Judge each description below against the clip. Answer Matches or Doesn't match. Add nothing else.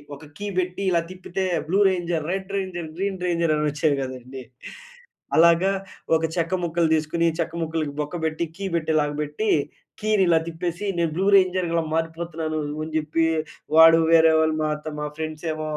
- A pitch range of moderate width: Doesn't match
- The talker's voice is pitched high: Doesn't match